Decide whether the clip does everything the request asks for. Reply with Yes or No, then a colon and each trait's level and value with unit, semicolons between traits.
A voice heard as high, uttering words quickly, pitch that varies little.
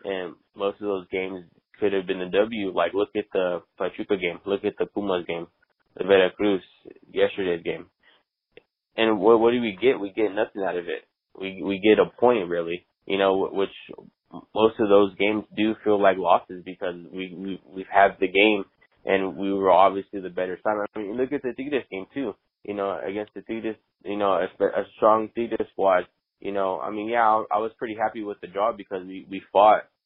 No: low, 100 Hz; fast, 215 wpm; narrow, 2.2 semitones